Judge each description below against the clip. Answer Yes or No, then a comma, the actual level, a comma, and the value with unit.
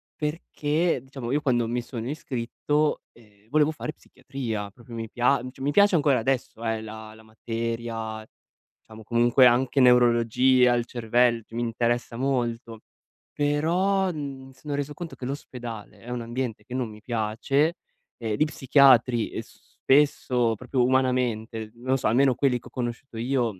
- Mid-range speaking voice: No, low, 125 Hz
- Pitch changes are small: No, average, 3.0 semitones